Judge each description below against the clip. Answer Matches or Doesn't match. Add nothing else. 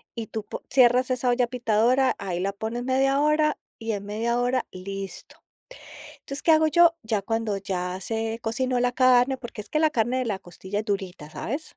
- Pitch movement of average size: Matches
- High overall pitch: Matches